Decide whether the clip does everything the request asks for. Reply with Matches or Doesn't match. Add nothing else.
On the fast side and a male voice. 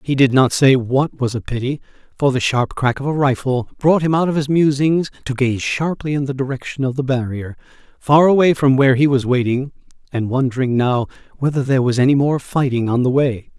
Matches